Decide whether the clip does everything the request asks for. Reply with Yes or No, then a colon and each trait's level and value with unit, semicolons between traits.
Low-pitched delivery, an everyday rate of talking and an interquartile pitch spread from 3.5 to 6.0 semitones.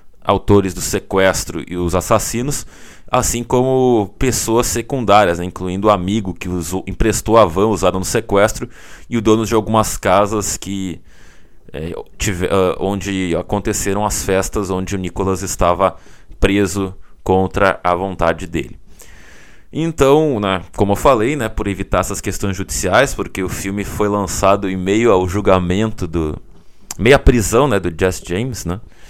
No: low, 100 Hz; average, 150 wpm; average, 2.8 semitones